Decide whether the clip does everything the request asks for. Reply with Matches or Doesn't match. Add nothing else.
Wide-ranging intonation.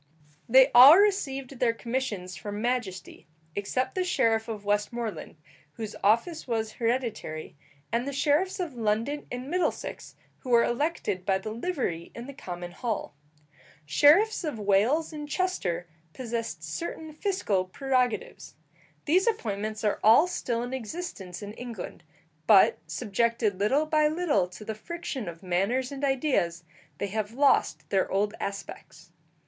Matches